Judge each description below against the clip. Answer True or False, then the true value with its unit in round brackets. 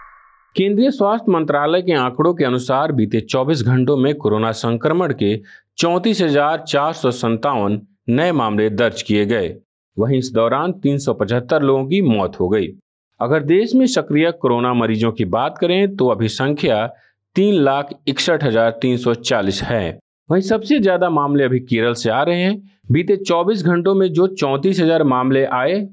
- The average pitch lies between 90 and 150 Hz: True (140 Hz)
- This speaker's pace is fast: False (155 wpm)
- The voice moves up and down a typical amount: False (6.9 semitones)